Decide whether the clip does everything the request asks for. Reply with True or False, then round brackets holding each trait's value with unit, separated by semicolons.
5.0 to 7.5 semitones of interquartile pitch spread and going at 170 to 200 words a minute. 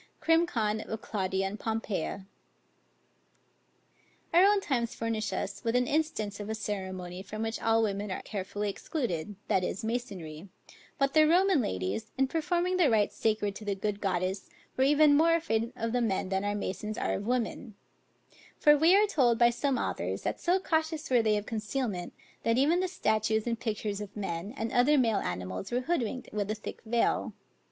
True (5.3 semitones; 180 wpm)